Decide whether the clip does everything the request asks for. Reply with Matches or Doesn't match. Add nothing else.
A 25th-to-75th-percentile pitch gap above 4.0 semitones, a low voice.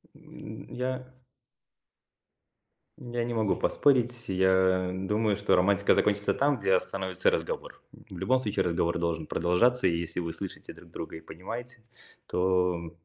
Matches